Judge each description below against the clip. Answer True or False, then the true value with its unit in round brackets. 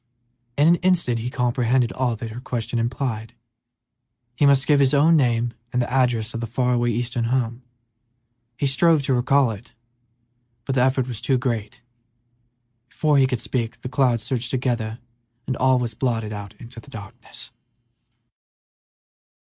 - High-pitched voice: False (125 Hz)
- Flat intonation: True (2.3 semitones)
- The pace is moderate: True (155 wpm)